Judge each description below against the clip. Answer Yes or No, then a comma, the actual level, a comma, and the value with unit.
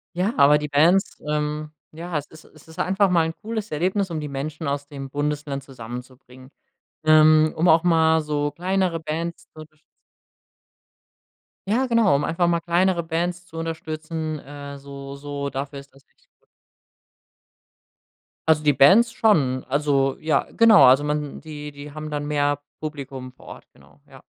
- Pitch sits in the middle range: Yes, medium, 155 Hz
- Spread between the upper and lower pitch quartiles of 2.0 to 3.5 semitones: Yes, average, 2.8 semitones